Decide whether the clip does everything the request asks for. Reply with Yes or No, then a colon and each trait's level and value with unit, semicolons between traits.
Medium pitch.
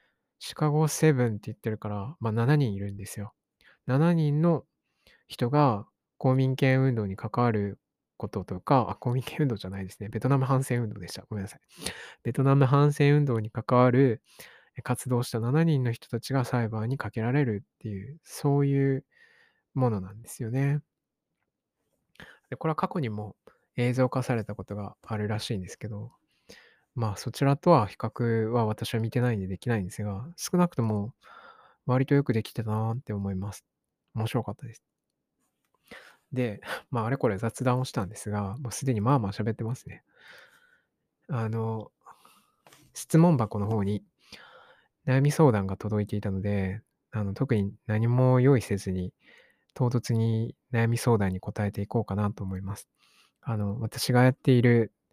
No: low, 115 Hz